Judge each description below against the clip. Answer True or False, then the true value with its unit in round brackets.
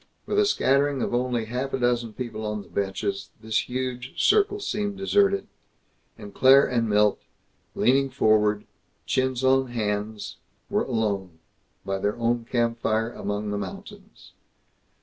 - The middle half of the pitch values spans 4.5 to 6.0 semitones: False (4.0 semitones)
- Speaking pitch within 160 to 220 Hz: False (120 Hz)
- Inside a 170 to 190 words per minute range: False (140 wpm)